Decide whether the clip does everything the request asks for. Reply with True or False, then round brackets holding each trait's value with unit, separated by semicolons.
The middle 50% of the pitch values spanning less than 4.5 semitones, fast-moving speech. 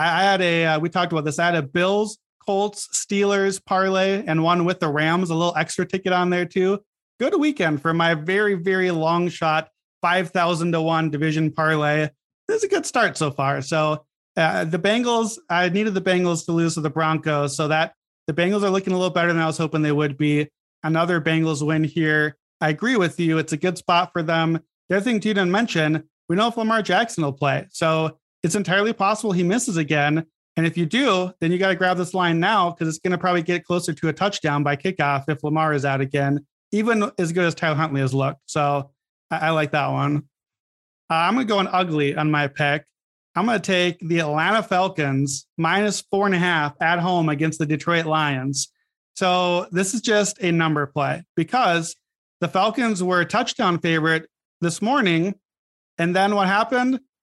True (3.4 semitones; 215 wpm)